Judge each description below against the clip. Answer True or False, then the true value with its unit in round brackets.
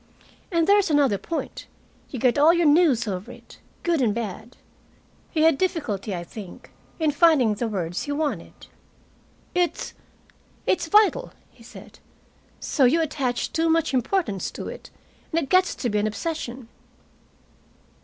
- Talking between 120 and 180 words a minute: True (150 wpm)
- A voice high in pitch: True (285 Hz)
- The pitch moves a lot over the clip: True (6.8 semitones)